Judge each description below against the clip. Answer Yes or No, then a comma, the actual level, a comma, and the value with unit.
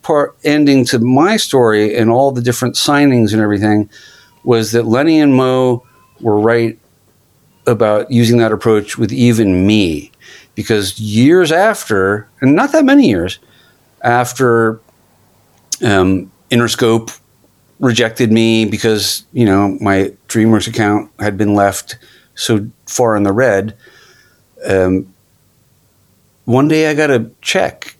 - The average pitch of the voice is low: Yes, low, 115 Hz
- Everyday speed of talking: No, slow, 125 wpm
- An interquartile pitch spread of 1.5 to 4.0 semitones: Yes, average, 3.2 semitones